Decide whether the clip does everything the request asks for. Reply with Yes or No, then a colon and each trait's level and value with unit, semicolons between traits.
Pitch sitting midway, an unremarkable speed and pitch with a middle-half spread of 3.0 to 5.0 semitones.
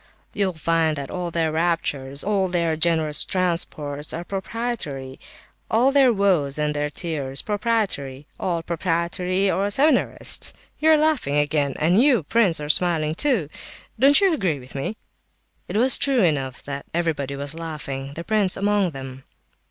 No: medium, 170 Hz; average, 150 wpm; wide, 5.5 semitones